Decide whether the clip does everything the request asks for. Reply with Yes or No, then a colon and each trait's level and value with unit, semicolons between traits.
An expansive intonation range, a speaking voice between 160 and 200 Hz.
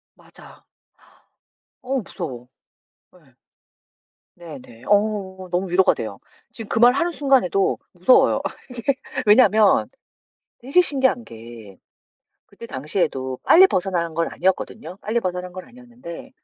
Yes: wide, 6.3 semitones; high, 190 Hz